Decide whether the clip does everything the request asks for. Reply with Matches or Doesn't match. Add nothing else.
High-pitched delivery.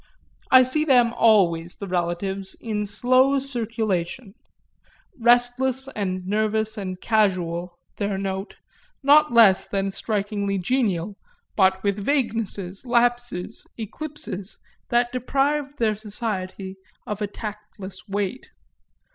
Matches